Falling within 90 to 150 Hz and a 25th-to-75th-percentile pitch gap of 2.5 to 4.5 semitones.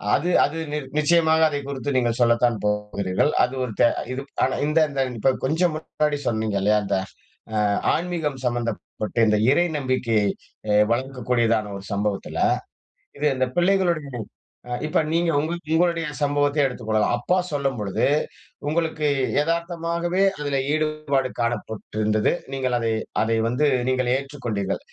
No: low, 135 Hz; average, 5.1 semitones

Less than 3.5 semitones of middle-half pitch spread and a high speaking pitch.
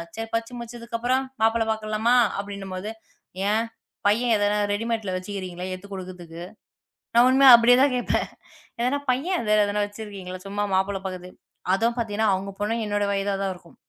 Yes: average, 3.0 semitones; high, 210 Hz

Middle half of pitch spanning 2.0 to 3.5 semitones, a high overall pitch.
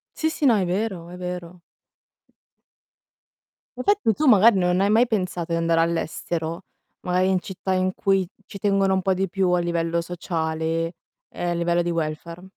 No: narrow, 2.4 semitones; medium, 180 Hz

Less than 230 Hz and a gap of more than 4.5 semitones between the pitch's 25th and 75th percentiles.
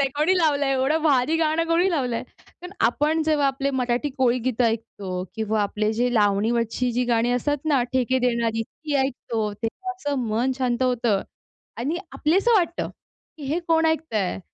No: very high, 260 Hz; average, 4.9 semitones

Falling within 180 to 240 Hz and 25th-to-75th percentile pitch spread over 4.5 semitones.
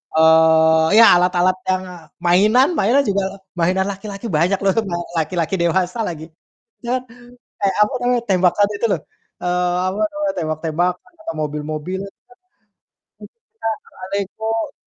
No: medium, 185 Hz; average, 3.4 semitones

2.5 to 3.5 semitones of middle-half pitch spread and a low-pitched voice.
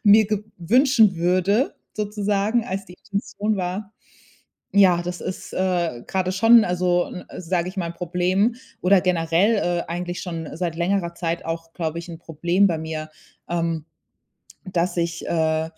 No: average, 2.9 semitones; medium, 180 Hz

